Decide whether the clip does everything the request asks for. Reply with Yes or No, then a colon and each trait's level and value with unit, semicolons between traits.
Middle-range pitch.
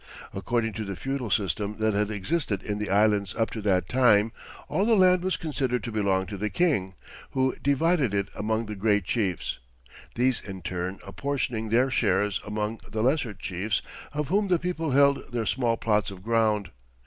No: low, 110 Hz